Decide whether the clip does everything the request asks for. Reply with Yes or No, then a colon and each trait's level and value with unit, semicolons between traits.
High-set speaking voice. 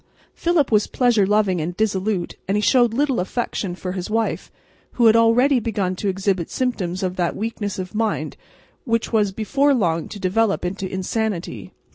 Yes: high, 210 Hz